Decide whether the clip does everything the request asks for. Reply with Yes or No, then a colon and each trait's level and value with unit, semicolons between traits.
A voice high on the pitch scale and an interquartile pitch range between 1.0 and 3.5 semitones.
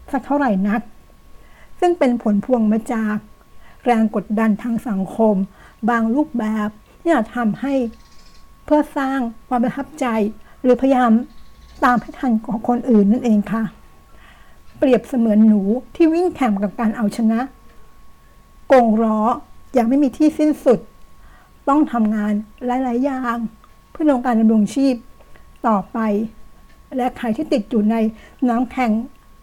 Yes: high, 235 Hz; average, 3.2 semitones